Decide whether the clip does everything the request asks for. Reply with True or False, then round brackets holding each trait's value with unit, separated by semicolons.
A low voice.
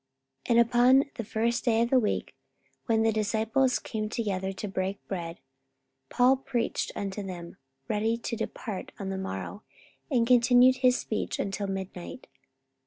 False (220 Hz)